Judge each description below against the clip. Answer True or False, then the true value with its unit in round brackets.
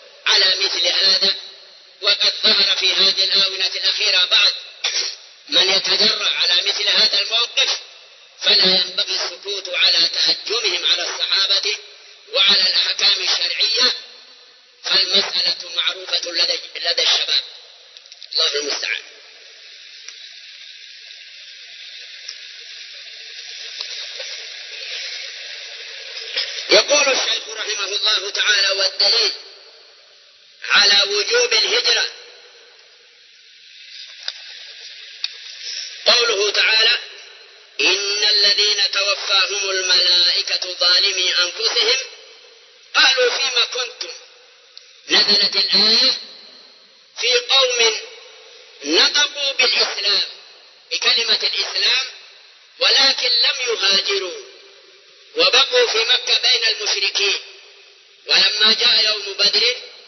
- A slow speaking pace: False (75 wpm)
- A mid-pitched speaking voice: False (290 Hz)